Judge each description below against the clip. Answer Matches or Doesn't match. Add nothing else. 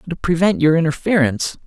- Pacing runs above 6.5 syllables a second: Doesn't match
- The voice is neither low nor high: Matches